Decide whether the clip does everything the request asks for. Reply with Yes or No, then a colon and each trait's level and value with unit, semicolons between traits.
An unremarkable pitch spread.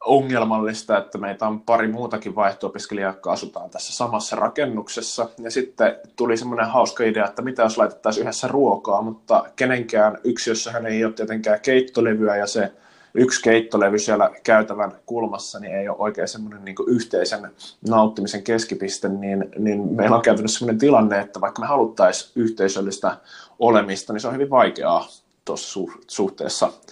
No: narrow, 2.1 semitones